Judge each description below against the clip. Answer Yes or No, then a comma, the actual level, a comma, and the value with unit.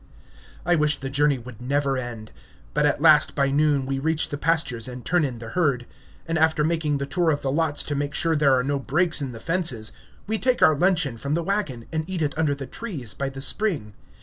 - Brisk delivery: Yes, fast, 230 wpm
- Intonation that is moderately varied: Yes, average, 3.3 semitones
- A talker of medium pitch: Yes, medium, 145 Hz